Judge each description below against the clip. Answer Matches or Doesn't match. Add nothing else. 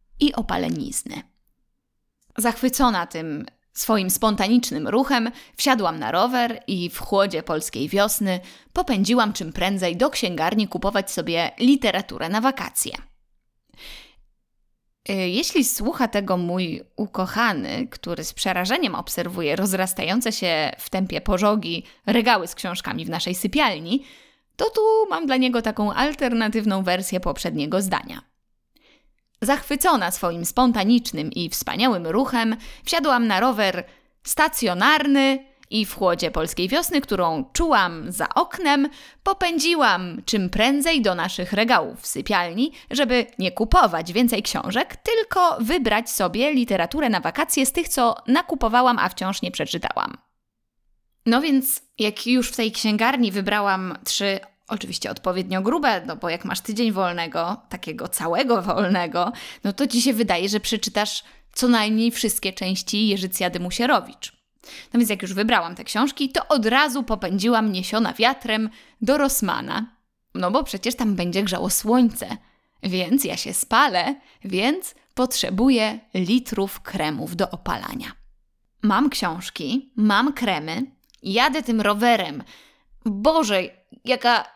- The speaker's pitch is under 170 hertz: Doesn't match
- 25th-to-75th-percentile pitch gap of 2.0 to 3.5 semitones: Doesn't match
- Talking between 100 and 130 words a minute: Matches